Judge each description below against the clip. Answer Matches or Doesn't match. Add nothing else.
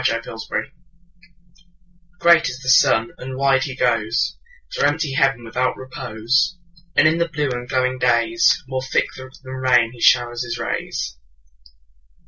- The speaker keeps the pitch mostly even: Doesn't match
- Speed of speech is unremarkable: Doesn't match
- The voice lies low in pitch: Matches